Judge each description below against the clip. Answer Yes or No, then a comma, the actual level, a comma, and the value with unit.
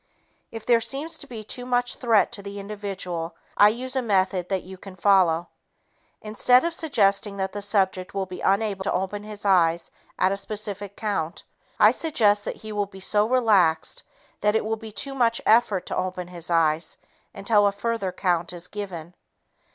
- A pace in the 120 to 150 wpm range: No, average, 185 wpm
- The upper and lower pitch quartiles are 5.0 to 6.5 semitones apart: No, average, 3.0 semitones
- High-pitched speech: Yes, high, 200 Hz